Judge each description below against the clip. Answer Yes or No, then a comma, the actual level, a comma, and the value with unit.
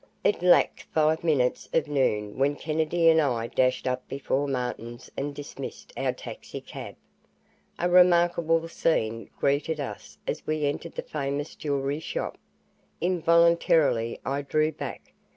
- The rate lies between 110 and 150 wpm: Yes, slow, 135 wpm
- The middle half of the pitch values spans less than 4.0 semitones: Yes, average, 3.4 semitones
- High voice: No, medium, 145 Hz